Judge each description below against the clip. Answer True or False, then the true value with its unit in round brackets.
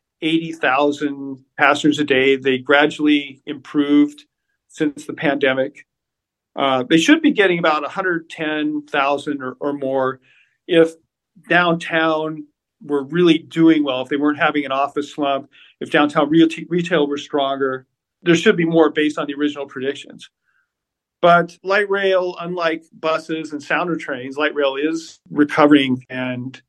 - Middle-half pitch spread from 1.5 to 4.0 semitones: True (2.7 semitones)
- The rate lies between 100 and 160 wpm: True (140 wpm)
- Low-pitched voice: False (150 Hz)